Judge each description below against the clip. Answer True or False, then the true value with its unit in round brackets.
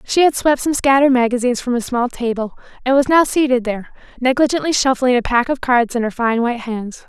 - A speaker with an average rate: False (220 wpm)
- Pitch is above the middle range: True (250 Hz)